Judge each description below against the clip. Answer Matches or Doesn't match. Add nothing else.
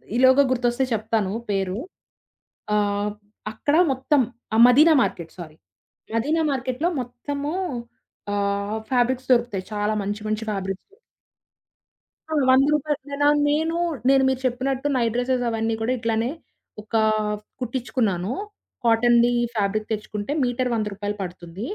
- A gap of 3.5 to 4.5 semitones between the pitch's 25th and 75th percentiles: Matches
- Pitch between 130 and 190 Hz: Doesn't match